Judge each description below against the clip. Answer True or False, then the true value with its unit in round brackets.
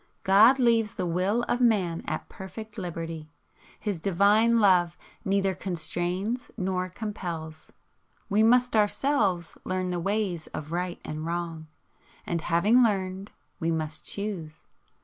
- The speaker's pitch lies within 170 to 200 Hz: True (185 Hz)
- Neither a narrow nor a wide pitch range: True (3.8 semitones)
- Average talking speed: False (130 wpm)